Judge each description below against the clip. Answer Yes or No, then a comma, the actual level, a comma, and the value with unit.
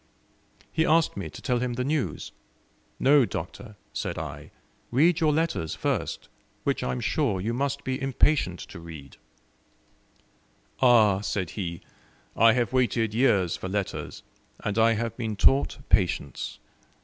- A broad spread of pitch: Yes, wide, 6.2 semitones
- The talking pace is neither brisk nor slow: Yes, average, 145 wpm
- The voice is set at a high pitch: No, low, 115 Hz